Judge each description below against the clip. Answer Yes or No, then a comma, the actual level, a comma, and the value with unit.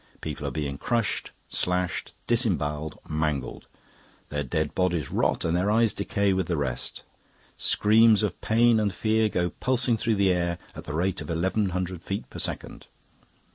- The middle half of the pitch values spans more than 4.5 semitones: Yes, average, 5.1 semitones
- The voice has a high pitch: No, very low, 90 Hz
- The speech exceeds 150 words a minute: Yes, average, 165 wpm